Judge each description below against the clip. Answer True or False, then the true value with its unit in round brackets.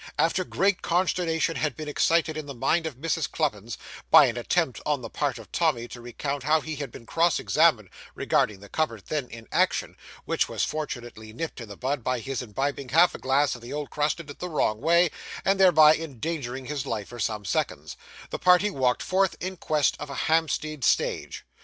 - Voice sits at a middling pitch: True (145 Hz)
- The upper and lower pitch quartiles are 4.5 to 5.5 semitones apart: True (4.9 semitones)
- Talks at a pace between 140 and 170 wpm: False (200 wpm)